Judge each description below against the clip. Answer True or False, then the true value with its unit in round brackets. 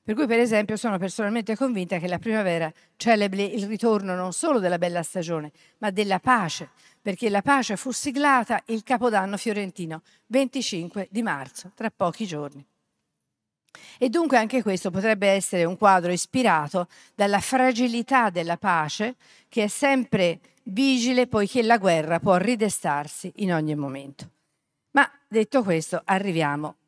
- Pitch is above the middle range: True (205 Hz)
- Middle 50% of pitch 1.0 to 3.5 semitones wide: False (5.0 semitones)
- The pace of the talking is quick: False (145 wpm)